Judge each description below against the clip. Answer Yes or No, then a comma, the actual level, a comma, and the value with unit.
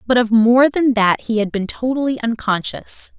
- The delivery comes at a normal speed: Yes, average, 190 wpm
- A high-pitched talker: Yes, high, 235 Hz